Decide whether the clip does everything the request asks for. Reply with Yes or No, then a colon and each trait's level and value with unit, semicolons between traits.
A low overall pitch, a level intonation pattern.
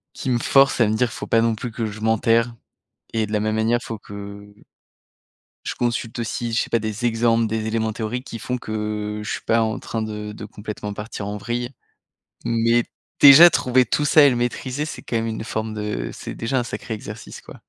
Yes: low, 115 Hz; narrow, 2.0 semitones